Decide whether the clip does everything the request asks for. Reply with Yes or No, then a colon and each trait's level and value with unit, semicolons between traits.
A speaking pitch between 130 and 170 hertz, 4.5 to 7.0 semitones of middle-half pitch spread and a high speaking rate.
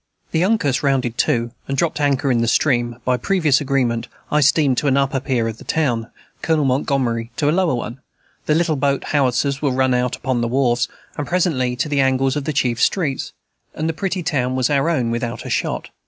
No: low, 135 Hz; average, 3.3 semitones; fast, 215 wpm